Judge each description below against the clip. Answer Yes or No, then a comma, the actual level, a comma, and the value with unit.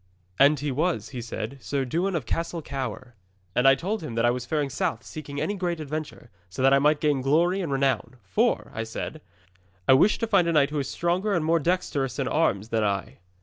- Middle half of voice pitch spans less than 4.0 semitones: No, average, 4.7 semitones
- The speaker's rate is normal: No, fast, 225 wpm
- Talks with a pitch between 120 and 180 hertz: Yes, medium, 140 Hz